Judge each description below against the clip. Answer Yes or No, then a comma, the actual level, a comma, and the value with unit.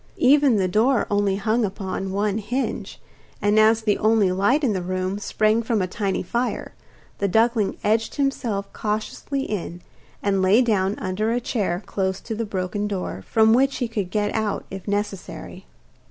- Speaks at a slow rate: No, average, 170 wpm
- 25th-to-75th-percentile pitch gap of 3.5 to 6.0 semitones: No, average, 2.7 semitones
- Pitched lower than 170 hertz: No, high, 210 Hz